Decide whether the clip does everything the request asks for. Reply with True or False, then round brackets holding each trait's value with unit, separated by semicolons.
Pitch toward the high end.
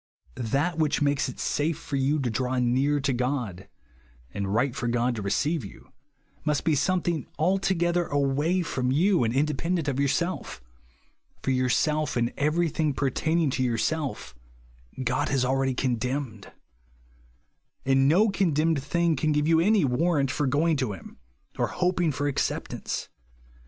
False (140 Hz)